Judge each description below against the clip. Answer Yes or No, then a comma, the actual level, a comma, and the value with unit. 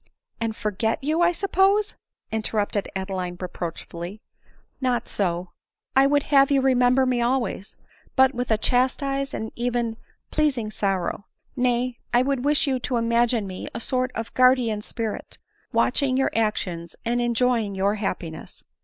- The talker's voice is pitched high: Yes, high, 240 Hz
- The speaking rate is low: No, average, 155 wpm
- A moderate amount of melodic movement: Yes, average, 3.9 semitones